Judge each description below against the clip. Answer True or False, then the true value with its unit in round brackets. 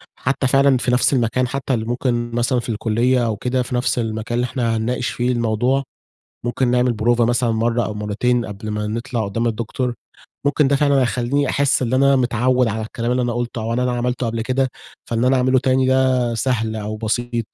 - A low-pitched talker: True (120 Hz)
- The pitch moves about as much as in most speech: False (2.0 semitones)